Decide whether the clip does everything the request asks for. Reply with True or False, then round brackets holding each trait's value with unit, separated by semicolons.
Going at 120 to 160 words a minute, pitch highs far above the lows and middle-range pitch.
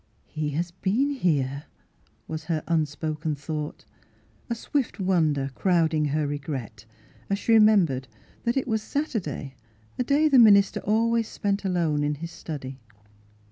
True (150 wpm; 6.6 semitones; 165 Hz)